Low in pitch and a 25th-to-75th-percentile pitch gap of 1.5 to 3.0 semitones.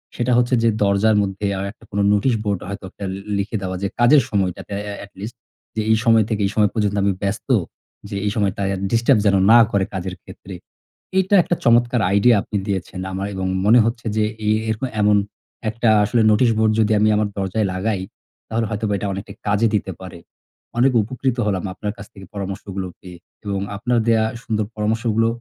Yes: low, 105 Hz; narrow, 2.6 semitones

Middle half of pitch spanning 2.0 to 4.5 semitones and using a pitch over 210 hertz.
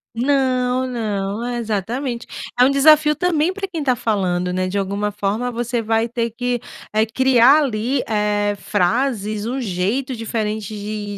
Yes: average, 3.7 semitones; high, 230 Hz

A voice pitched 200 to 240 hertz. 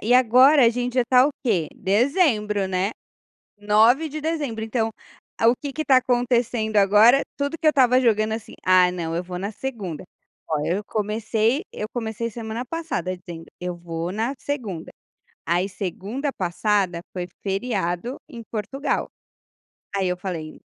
Yes: high, 220 Hz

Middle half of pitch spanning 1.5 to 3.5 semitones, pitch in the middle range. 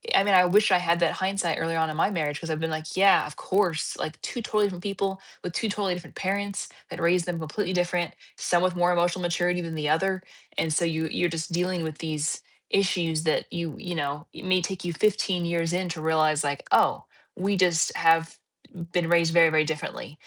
Yes: narrow, 2.4 semitones; medium, 175 Hz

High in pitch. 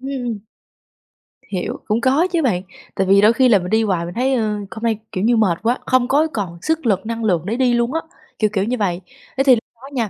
Yes: high, 225 Hz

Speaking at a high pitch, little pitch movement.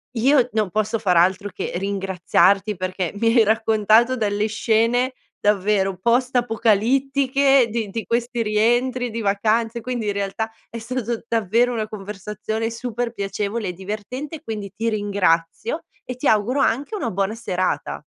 No: high, 220 Hz; average, 3.0 semitones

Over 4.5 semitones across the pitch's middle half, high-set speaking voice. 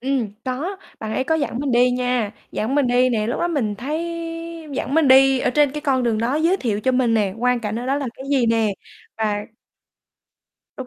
No: average, 3.4 semitones; very high, 250 Hz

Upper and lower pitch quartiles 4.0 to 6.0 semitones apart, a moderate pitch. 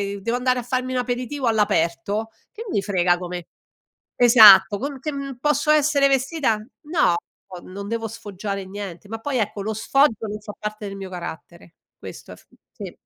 No: average, 4.6 semitones; high, 220 Hz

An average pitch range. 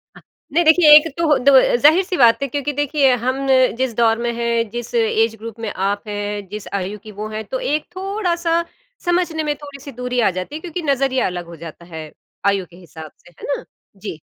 No: wide, 6.1 semitones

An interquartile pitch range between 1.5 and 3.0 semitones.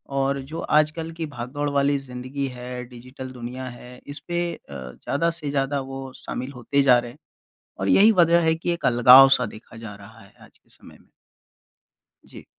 Yes: average, 2.7 semitones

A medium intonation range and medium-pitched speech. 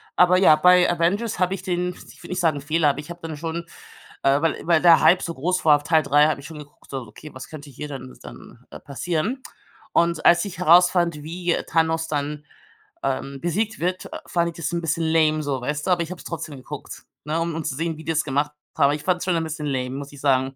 Yes: average, 3.0 semitones; medium, 160 Hz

